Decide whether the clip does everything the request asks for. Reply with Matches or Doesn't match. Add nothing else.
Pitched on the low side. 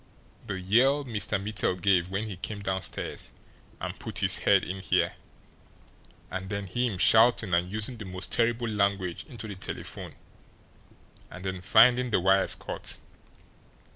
Matches